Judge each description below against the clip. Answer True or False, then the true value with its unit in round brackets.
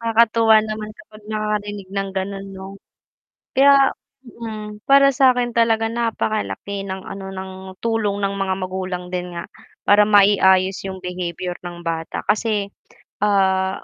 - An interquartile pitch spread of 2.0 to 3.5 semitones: True (2.8 semitones)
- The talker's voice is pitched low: False (205 Hz)